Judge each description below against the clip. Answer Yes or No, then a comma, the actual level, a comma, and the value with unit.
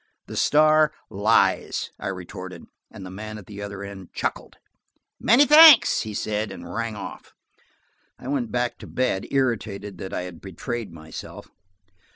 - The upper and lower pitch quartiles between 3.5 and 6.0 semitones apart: Yes, average, 4.5 semitones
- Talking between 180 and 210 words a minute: No, average, 155 wpm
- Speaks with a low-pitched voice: Yes, low, 105 Hz